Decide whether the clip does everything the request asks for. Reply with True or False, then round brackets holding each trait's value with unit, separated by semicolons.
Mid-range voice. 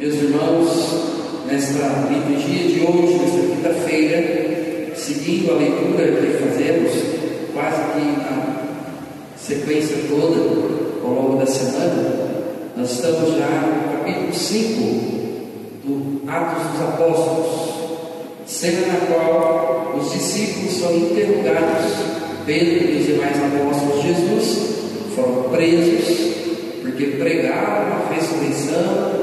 True (160 Hz)